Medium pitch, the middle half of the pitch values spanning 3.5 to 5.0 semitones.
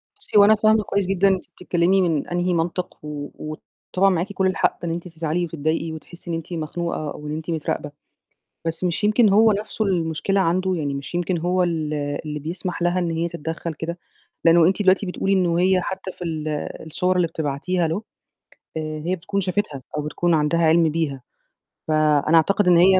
No: medium, 170 Hz; average, 2.8 semitones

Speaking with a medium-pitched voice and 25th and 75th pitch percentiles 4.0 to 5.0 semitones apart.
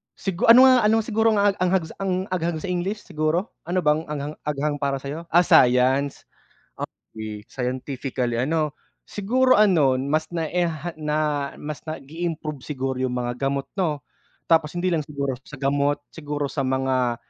Yes: medium, 150 Hz; average, 4.4 semitones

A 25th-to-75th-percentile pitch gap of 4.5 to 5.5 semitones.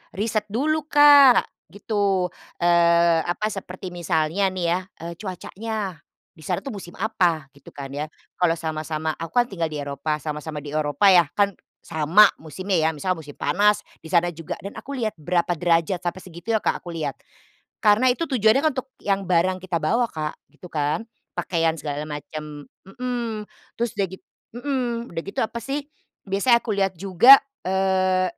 Yes: average, 5.0 semitones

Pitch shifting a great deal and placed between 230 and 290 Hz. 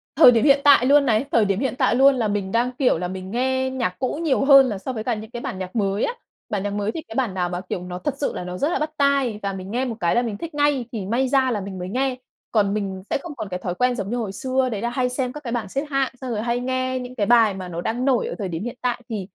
No: average, 4.8 semitones; high, 235 Hz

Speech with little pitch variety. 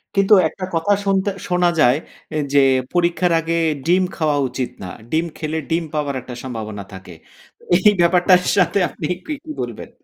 No: average, 4.3 semitones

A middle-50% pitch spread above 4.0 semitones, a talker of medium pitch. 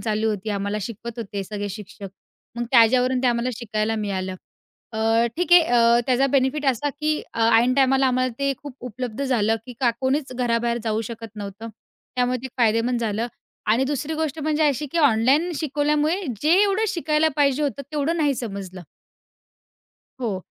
No: average, 4.5 semitones; very high, 250 Hz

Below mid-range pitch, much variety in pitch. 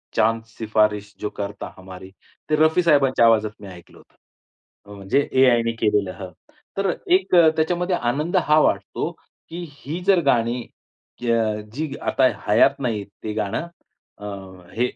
Yes: low, 120 Hz; wide, 6.8 semitones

